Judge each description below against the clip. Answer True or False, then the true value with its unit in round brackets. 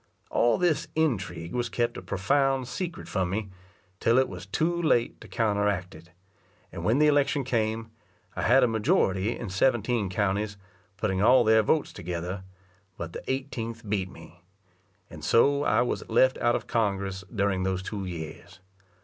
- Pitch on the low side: True (110 Hz)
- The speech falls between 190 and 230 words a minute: False (165 wpm)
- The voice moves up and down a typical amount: True (4.8 semitones)